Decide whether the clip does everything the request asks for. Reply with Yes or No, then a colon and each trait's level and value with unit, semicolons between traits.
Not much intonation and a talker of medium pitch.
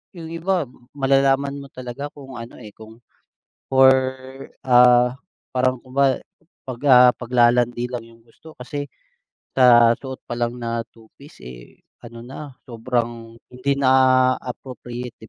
No: narrow, 2.2 semitones; low, 125 Hz